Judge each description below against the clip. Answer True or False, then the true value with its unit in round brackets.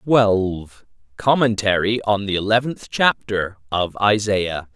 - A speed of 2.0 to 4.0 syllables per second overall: True (3.8 syllables/s)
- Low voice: True (105 Hz)